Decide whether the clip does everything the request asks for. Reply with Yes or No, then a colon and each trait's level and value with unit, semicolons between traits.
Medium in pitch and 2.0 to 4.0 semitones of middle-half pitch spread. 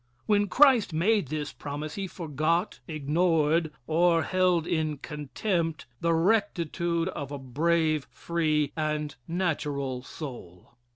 Yes: medium, 160 Hz; average, 2.7 semitones